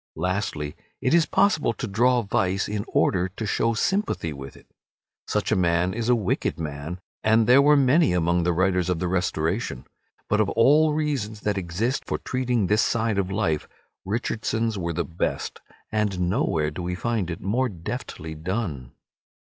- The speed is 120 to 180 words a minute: Yes, average, 170 wpm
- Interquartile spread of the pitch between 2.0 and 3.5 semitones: No, average, 5.1 semitones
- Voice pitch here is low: Yes, low, 100 Hz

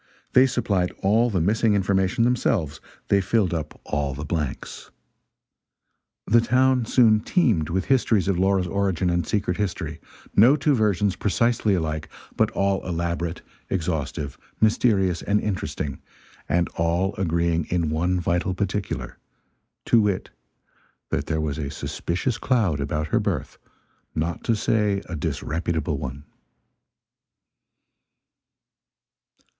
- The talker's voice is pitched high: No, very low, 95 Hz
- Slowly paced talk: Yes, slow, 125 wpm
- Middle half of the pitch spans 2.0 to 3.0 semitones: No, average, 4.5 semitones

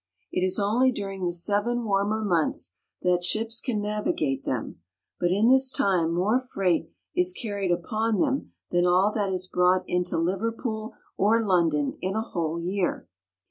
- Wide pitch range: No, average, 3.7 semitones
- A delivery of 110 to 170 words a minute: Yes, average, 165 wpm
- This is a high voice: Yes, high, 195 Hz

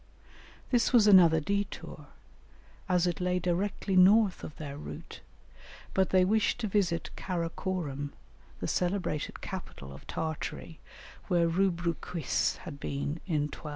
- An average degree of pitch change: Yes, average, 3.3 semitones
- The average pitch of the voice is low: No, medium, 175 Hz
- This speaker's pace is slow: Yes, slow, 130 wpm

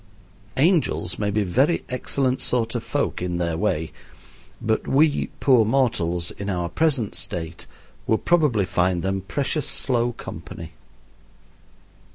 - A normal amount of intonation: No, wide, 7.1 semitones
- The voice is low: Yes, low, 110 Hz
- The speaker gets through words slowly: Yes, slow, 130 wpm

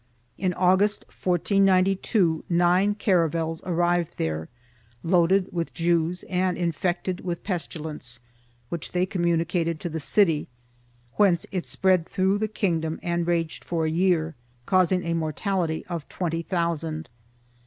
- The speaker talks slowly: Yes, slow, 125 wpm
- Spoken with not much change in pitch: Yes, narrow, 2.2 semitones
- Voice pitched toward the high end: No, medium, 175 Hz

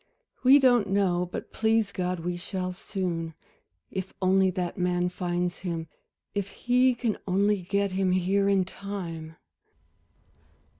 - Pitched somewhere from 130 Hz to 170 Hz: No, medium, 185 Hz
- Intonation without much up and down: Yes, narrow, 2.1 semitones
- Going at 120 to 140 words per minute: Yes, slow, 135 wpm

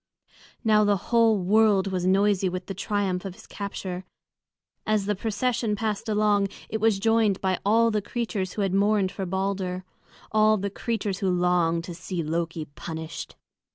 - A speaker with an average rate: Yes, average, 165 wpm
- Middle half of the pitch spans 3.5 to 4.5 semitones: No, average, 2.7 semitones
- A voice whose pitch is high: Yes, high, 200 Hz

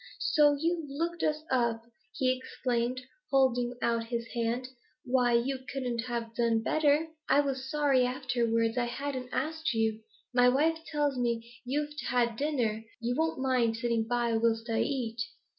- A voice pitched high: Yes, very high, 250 Hz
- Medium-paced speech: Yes, average, 155 wpm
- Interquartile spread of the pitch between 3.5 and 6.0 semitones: No, average, 3.1 semitones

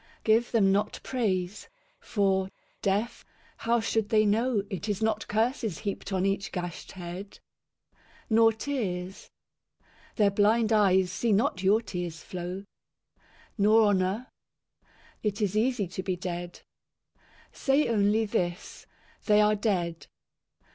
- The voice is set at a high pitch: Yes, high, 205 Hz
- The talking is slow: Yes, slow, 125 wpm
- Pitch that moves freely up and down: No, average, 2.9 semitones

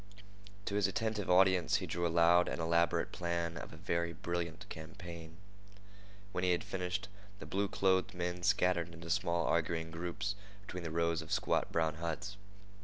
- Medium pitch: No, very low, 85 Hz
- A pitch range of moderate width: No, narrow, 1.7 semitones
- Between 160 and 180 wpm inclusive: Yes, average, 170 wpm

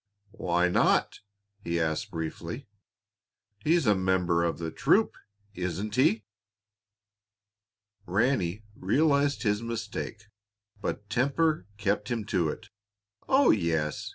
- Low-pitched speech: Yes, low, 105 Hz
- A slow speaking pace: Yes, slow, 105 wpm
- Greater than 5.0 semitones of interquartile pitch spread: Yes, wide, 5.6 semitones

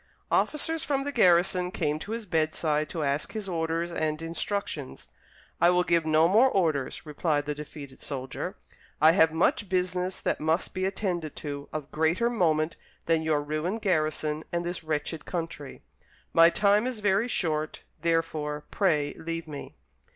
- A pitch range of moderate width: Yes, average, 3.3 semitones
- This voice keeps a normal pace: Yes, average, 160 wpm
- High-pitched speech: No, medium, 165 Hz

